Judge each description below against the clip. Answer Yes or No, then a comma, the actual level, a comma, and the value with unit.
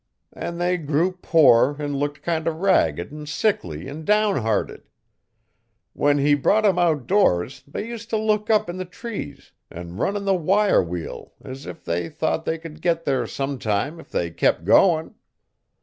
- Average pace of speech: Yes, average, 170 wpm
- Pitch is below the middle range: No, medium, 155 Hz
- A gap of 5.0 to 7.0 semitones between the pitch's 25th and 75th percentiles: Yes, wide, 5.5 semitones